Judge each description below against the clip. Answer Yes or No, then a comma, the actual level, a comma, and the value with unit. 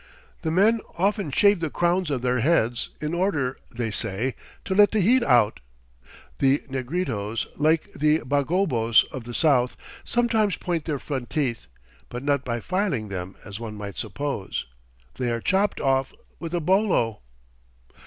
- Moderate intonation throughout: No, wide, 7.0 semitones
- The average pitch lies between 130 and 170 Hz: Yes, medium, 140 Hz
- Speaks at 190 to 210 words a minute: No, average, 155 wpm